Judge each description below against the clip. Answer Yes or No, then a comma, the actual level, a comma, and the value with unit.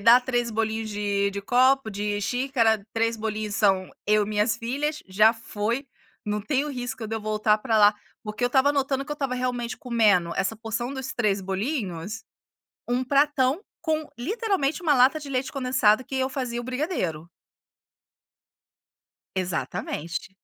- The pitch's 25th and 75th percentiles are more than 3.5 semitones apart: Yes, average, 4.0 semitones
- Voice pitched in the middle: No, high, 235 Hz